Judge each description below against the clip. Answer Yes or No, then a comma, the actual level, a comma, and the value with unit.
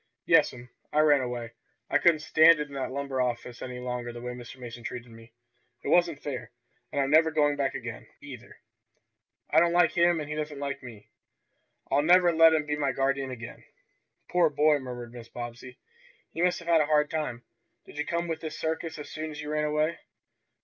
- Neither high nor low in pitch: Yes, medium, 145 Hz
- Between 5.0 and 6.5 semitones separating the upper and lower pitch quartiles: No, average, 4.1 semitones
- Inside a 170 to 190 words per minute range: No, fast, 205 wpm